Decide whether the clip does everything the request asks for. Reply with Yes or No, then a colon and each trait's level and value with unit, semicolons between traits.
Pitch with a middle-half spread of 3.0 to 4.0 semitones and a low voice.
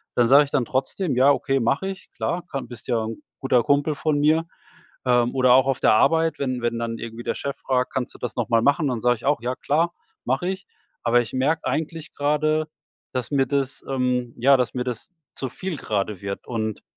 Yes: average, 3.4 semitones; low, 130 Hz